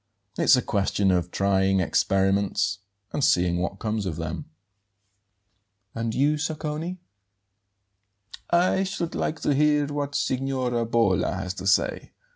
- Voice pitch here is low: Yes, low, 115 Hz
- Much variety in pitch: Yes, wide, 7.3 semitones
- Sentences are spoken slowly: Yes, slow, 125 wpm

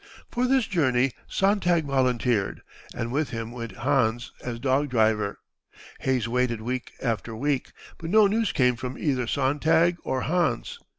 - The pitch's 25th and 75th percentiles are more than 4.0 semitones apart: Yes, average, 4.9 semitones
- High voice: No, low, 130 Hz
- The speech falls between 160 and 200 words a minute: No, average, 145 wpm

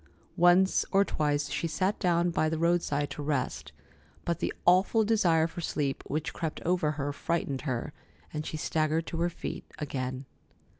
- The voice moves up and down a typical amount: Yes, average, 3.0 semitones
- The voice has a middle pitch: Yes, medium, 160 Hz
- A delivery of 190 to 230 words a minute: No, average, 165 wpm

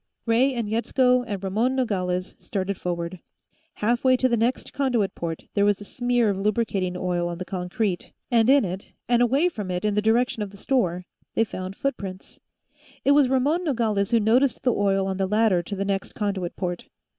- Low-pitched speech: No, high, 210 Hz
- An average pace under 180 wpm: No, average, 195 wpm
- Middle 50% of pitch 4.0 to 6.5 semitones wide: Yes, average, 4.5 semitones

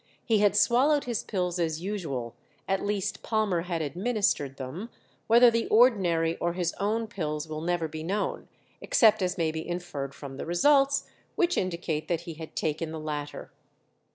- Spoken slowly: No, average, 170 wpm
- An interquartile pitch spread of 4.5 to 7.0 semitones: Yes, average, 5.1 semitones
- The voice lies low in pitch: No, medium, 175 Hz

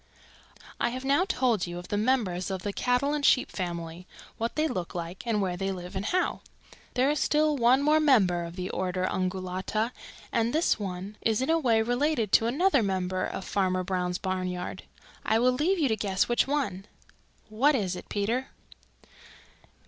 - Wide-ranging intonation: Yes, wide, 6.0 semitones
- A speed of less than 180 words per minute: No, average, 185 wpm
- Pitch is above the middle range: Yes, high, 215 Hz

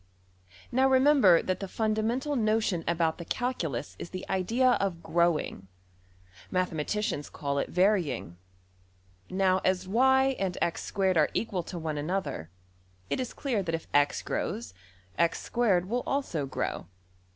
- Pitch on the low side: No, medium, 185 Hz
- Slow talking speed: Yes, slow, 120 wpm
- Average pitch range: No, wide, 5.7 semitones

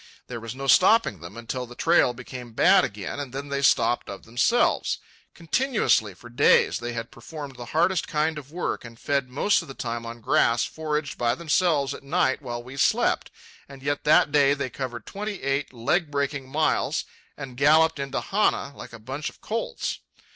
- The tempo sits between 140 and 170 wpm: No, average, 190 wpm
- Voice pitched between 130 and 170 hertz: Yes, low, 135 Hz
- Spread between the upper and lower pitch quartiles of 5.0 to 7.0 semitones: No, average, 4.2 semitones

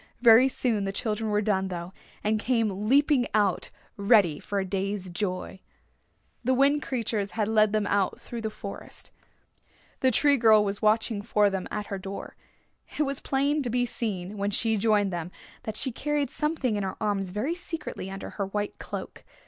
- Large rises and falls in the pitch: No, average, 3.6 semitones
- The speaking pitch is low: No, high, 215 Hz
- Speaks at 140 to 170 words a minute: No, average, 180 wpm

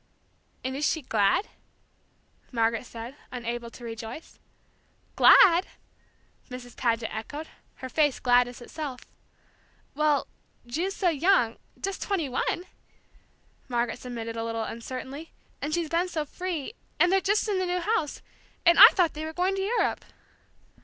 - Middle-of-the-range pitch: No, very high, 290 Hz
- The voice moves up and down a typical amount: No, wide, 6.6 semitones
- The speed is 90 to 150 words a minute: Yes, average, 140 wpm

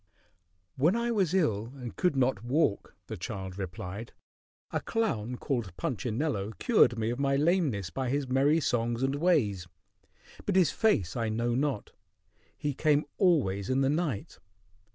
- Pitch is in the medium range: No, low, 130 Hz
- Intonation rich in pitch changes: Yes, wide, 6.1 semitones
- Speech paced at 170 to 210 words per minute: No, average, 155 wpm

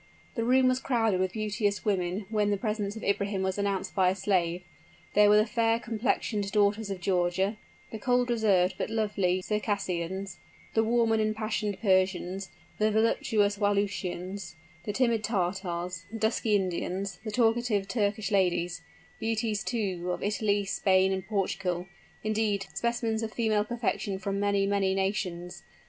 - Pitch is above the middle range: Yes, high, 205 Hz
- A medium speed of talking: Yes, average, 150 wpm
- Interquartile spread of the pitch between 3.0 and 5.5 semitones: No, narrow, 2.5 semitones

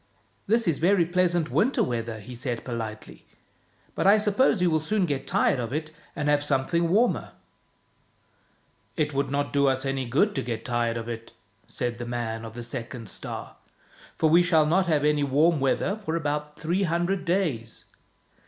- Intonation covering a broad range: Yes, wide, 6.1 semitones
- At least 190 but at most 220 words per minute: Yes, average, 195 wpm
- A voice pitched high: No, medium, 150 Hz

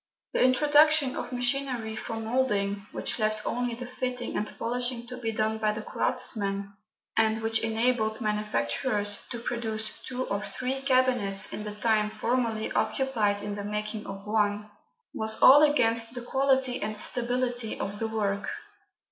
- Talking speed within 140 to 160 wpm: Yes, average, 155 wpm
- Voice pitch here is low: No, high, 225 Hz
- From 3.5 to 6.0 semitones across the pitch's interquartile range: No, average, 2.9 semitones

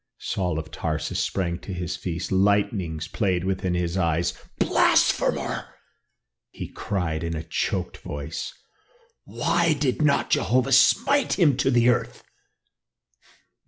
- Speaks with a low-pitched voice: Yes, very low, 95 Hz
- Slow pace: Yes, slow, 125 wpm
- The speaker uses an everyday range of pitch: No, wide, 7.0 semitones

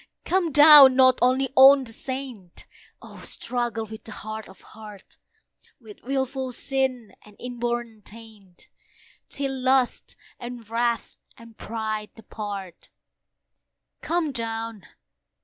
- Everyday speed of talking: No, slow, 115 wpm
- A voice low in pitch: No, high, 235 Hz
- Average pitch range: Yes, average, 3.3 semitones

